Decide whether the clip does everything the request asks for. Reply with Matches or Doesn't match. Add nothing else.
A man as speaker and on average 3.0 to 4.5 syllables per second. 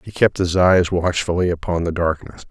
Doesn't match